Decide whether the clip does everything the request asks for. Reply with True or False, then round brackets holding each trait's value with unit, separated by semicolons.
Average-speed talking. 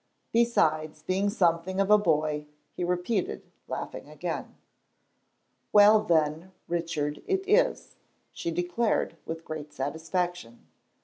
False (110 wpm)